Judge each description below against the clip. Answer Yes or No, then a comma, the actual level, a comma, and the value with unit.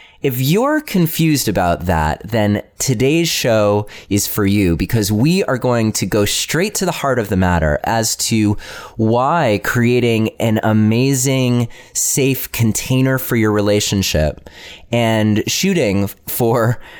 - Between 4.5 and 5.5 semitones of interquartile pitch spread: No, average, 4.1 semitones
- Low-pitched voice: Yes, low, 115 Hz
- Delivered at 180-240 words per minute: No, slow, 135 wpm